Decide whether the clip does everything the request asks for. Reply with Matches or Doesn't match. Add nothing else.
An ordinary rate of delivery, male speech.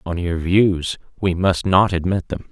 Matches